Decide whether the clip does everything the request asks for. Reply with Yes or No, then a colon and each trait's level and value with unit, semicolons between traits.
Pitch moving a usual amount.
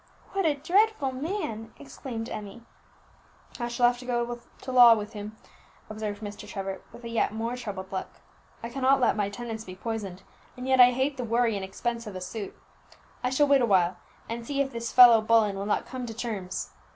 Yes: average, 3.2 semitones